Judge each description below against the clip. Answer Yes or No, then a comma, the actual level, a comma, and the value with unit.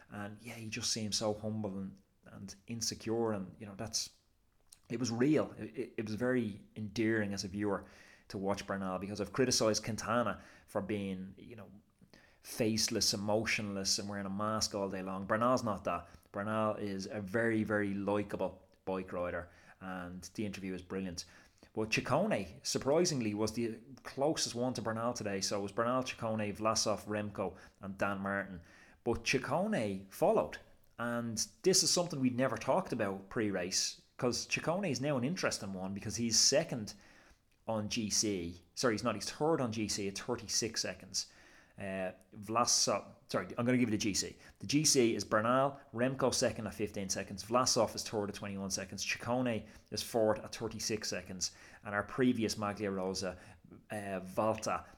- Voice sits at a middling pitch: No, low, 105 Hz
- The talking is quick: No, average, 165 wpm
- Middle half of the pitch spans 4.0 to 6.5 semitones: No, average, 2.8 semitones